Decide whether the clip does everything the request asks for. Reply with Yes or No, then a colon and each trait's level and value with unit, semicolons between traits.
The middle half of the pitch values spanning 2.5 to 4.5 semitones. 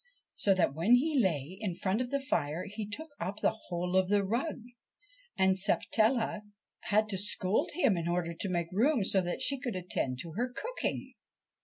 No: average, 5.2 semitones